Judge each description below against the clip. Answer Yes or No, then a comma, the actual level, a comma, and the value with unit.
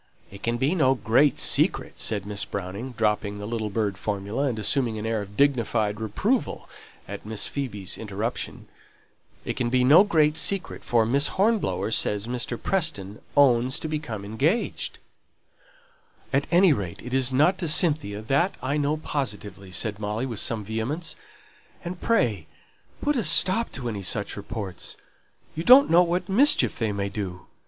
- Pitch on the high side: No, low, 120 Hz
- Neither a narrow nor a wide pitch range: No, wide, 6.8 semitones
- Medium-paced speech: Yes, average, 150 wpm